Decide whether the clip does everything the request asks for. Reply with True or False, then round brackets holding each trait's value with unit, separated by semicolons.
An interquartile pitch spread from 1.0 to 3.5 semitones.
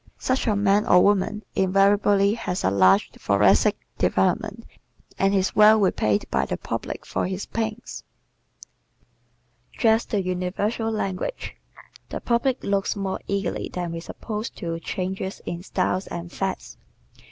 True (2.5 semitones)